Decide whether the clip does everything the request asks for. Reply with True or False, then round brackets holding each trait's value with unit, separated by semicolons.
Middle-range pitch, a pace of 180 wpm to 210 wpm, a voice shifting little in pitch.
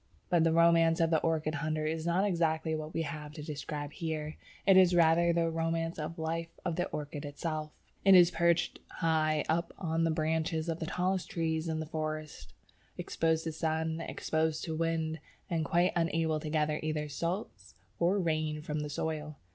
True (160 Hz; 185 wpm; 1.3 semitones)